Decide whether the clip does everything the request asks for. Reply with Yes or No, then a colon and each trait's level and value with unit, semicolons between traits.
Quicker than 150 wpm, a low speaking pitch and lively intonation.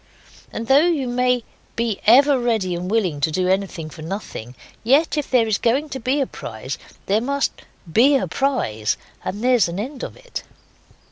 No: average, 180 wpm; high, 230 Hz; wide, 6.4 semitones